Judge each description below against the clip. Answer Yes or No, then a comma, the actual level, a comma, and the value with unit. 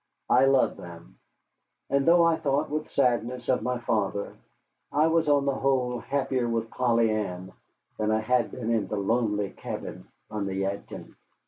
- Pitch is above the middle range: No, low, 120 Hz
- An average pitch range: Yes, average, 4.4 semitones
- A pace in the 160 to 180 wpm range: Yes, average, 165 wpm